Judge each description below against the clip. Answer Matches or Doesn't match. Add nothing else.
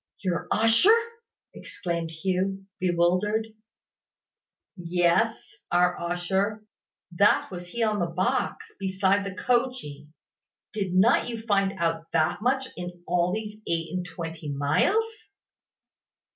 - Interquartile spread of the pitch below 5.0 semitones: Matches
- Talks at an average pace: Doesn't match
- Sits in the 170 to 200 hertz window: Matches